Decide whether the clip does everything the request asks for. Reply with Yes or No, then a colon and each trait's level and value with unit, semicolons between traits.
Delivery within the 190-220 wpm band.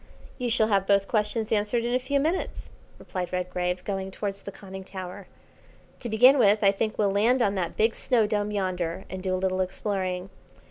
Yes: average, 195 wpm